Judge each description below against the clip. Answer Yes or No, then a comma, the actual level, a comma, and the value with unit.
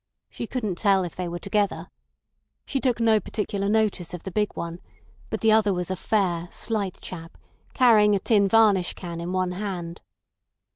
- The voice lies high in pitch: Yes, high, 195 Hz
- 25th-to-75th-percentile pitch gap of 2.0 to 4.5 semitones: Yes, average, 3.3 semitones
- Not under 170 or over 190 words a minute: Yes, average, 180 wpm